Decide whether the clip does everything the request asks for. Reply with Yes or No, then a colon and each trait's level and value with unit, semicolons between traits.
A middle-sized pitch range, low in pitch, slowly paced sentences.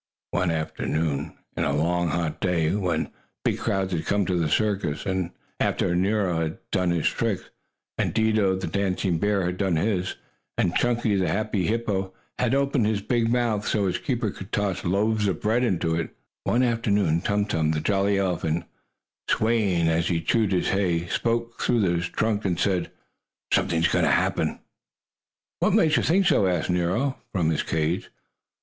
No: average, 4.1 semitones; very low, 95 Hz; average, 175 wpm